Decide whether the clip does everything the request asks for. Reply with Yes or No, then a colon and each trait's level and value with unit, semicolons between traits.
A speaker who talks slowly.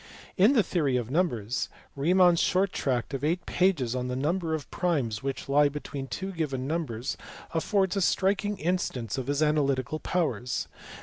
No: average, 170 wpm